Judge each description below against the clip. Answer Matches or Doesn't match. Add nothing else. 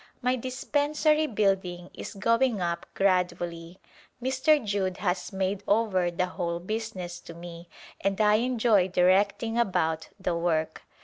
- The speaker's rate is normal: Doesn't match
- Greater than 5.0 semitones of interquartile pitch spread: Doesn't match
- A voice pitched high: Matches